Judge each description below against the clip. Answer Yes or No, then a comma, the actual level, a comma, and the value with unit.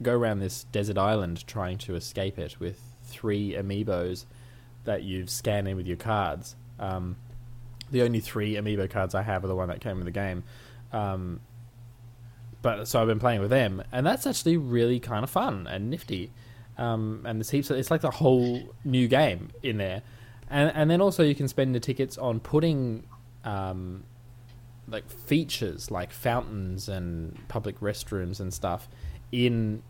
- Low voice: Yes, low, 115 Hz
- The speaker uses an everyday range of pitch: Yes, average, 3.7 semitones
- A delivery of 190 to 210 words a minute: No, average, 175 wpm